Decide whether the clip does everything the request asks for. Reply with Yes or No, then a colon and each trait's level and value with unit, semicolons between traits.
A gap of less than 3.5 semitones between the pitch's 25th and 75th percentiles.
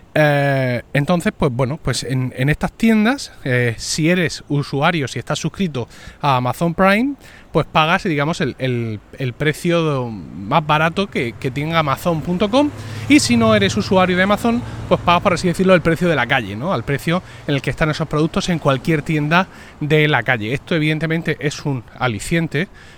No: average, 4.8 semitones